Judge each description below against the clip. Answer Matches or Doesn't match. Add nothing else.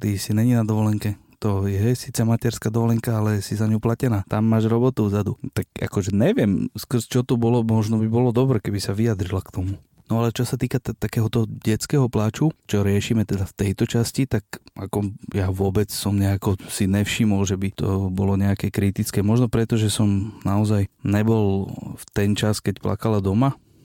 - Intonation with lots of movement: Doesn't match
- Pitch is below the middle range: Matches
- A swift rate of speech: Matches